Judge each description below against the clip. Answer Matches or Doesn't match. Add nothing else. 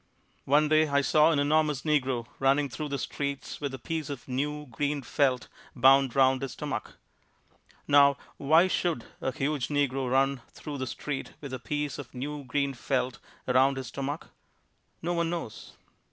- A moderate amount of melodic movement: Doesn't match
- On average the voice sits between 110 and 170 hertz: Matches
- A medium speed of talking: Matches